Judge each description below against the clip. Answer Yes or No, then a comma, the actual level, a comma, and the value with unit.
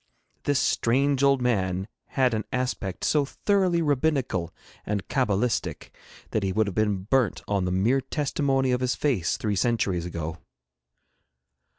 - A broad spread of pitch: Yes, wide, 5.8 semitones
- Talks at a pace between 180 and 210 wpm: No, average, 145 wpm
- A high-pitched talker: No, low, 120 Hz